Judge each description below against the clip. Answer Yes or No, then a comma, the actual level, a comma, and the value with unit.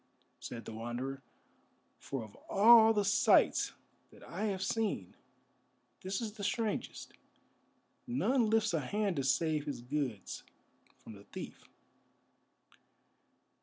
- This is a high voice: No, medium, 170 Hz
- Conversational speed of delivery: No, slow, 120 wpm